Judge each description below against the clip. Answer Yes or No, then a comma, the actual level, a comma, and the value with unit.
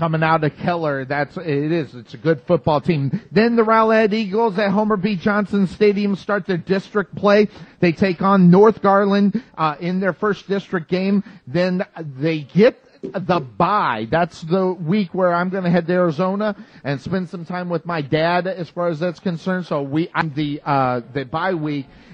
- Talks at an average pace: Yes, average, 190 wpm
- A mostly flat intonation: No, average, 3.8 semitones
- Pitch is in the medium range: Yes, medium, 180 Hz